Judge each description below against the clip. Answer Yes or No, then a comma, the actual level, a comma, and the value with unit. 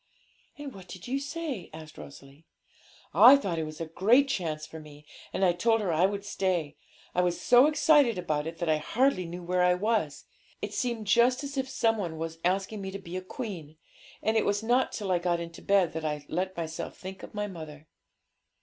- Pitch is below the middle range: No, medium, 185 Hz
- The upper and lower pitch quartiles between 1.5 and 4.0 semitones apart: No, wide, 5.5 semitones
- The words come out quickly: Yes, fast, 215 wpm